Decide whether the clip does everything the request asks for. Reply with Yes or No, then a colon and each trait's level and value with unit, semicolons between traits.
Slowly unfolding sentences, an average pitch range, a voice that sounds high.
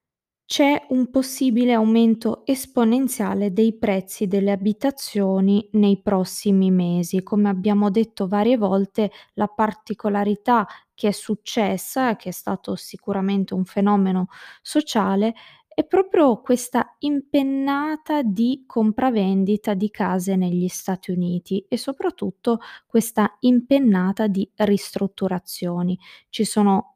Yes: slow, 105 wpm; average, 3.9 semitones; high, 210 Hz